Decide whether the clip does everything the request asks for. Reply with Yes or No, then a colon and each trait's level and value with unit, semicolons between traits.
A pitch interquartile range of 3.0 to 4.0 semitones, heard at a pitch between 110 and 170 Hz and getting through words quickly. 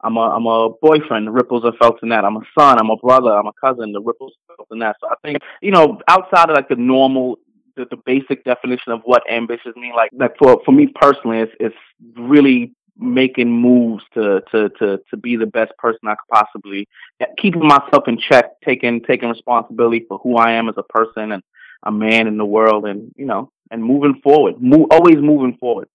Yes: average, 3.4 semitones; low, 120 Hz; fast, 220 wpm